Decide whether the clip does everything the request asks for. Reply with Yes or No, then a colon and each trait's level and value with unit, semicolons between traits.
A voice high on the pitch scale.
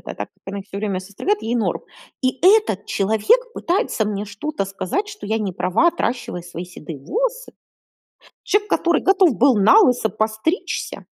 Yes: high, 225 Hz